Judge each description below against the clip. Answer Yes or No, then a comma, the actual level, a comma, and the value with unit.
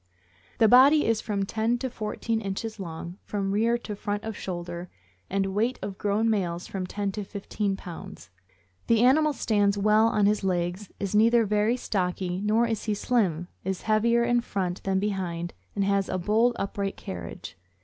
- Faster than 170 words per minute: Yes, average, 180 wpm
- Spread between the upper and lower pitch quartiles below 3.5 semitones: Yes, average, 2.8 semitones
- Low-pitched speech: No, high, 205 Hz